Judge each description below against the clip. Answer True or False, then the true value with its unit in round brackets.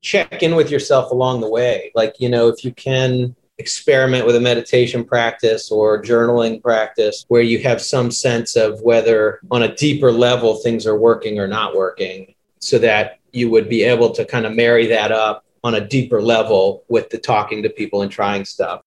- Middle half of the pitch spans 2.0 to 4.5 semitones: True (2.4 semitones)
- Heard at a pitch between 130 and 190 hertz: False (120 Hz)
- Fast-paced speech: False (195 wpm)